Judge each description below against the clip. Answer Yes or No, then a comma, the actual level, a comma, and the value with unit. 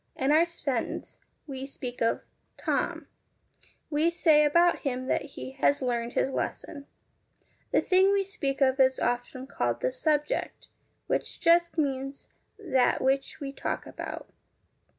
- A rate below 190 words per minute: Yes, average, 150 wpm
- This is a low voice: No, very high, 280 Hz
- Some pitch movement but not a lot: Yes, average, 4.2 semitones